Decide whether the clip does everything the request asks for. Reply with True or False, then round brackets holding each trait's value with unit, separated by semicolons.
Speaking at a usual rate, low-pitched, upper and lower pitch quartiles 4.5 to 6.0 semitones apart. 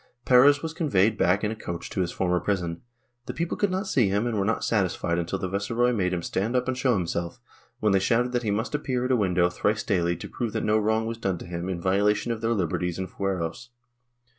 False (240 wpm; 105 Hz; 4.9 semitones)